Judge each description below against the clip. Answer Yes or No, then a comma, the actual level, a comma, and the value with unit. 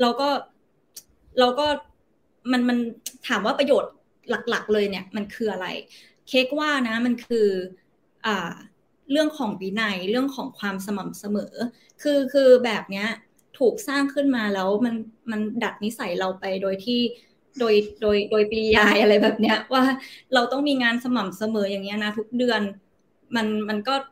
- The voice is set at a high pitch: Yes, high, 225 Hz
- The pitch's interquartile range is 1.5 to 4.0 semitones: Yes, average, 3.6 semitones